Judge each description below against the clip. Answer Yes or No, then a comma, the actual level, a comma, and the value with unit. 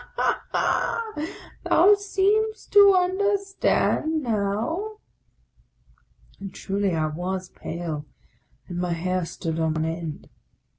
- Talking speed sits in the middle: No, slow, 100 wpm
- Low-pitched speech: No, high, 200 Hz